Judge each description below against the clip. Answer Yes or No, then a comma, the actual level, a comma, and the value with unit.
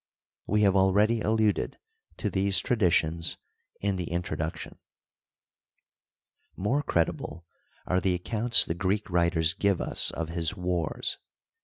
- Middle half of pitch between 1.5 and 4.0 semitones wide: Yes, average, 3.5 semitones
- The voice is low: Yes, very low, 95 Hz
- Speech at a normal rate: No, slow, 120 wpm